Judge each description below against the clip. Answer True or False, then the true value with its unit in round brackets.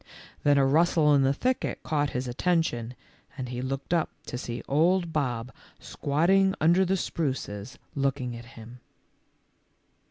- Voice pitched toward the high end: False (140 Hz)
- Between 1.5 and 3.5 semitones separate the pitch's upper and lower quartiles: False (4.9 semitones)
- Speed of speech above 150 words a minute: False (145 wpm)